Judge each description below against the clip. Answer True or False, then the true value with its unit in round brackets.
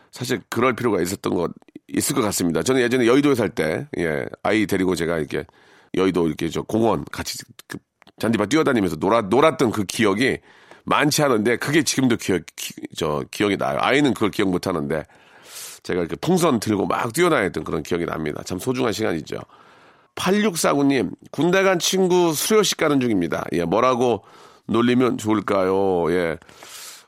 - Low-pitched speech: True (120 Hz)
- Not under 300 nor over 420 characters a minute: True (345 characters per minute)